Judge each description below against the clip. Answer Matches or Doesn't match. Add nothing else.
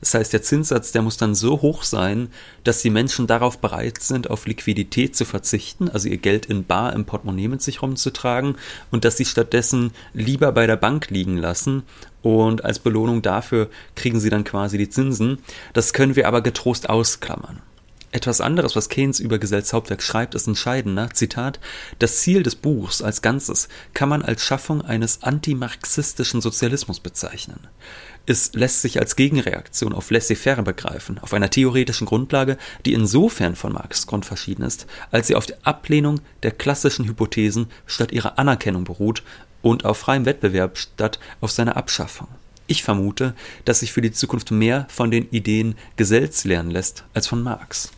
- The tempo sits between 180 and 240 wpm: Doesn't match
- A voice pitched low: Matches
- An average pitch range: Matches